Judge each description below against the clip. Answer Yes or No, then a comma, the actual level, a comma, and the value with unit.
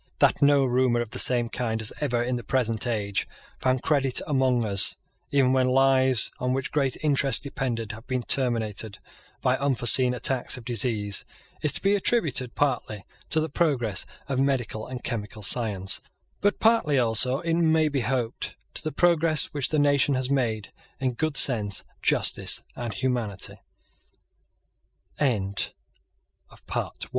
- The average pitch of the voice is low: Yes, low, 130 Hz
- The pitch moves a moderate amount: Yes, average, 3.5 semitones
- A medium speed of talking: Yes, average, 150 wpm